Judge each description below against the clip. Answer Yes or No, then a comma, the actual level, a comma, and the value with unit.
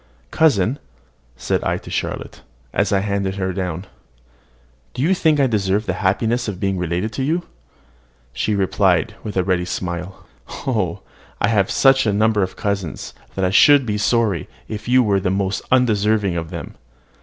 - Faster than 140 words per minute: Yes, average, 170 wpm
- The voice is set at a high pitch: No, low, 100 Hz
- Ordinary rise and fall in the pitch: Yes, average, 3.5 semitones